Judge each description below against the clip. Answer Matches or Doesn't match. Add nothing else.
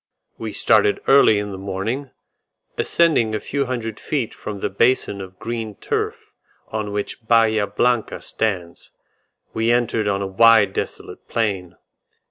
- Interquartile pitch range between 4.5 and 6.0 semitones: Doesn't match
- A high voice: Doesn't match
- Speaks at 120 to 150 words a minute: Matches